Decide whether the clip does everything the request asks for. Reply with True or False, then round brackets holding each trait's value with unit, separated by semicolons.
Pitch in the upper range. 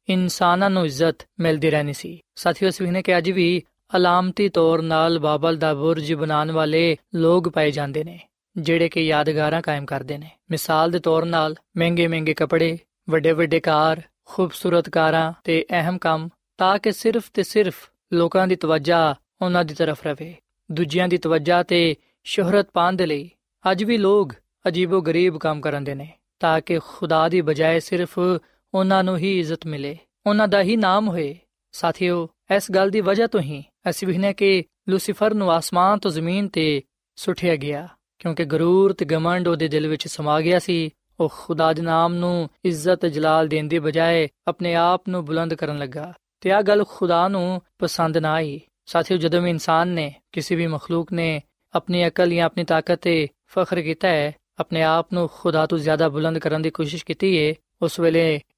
False (170 Hz)